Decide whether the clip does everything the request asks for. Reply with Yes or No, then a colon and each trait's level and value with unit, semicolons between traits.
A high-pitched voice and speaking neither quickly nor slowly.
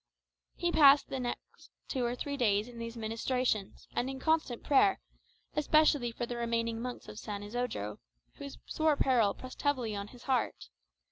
Yes: high, 245 Hz; average, 165 wpm